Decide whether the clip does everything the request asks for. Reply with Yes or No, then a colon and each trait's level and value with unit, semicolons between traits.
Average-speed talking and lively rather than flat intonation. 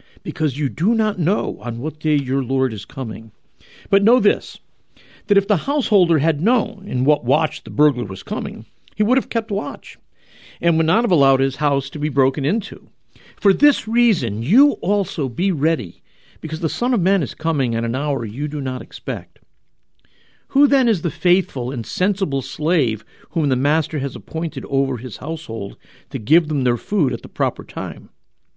Yes: average, 190 wpm; wide, 6.7 semitones